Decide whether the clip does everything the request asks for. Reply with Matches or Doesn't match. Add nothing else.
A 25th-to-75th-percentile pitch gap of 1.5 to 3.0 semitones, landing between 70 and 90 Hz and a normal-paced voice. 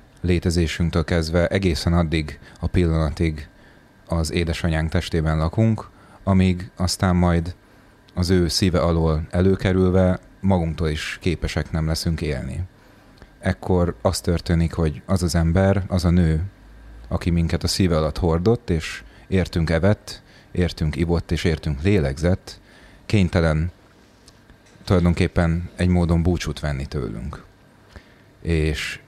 Matches